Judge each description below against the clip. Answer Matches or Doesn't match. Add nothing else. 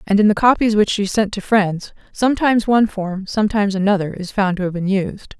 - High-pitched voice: Matches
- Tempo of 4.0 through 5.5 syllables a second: Doesn't match